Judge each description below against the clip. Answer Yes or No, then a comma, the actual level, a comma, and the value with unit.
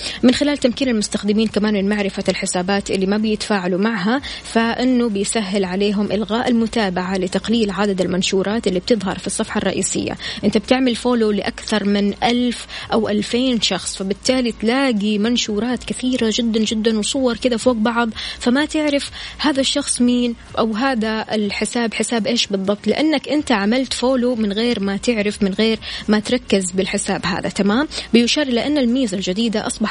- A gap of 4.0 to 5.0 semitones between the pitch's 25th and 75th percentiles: No, average, 3.2 semitones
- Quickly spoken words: Yes, fast, 155 wpm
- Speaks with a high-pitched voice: Yes, high, 220 Hz